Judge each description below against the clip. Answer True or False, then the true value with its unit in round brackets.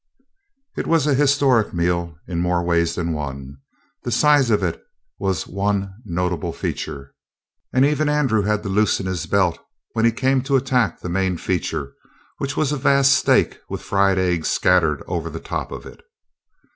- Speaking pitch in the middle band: False (100 Hz)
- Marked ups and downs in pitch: True (7.2 semitones)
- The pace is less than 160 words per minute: False (170 wpm)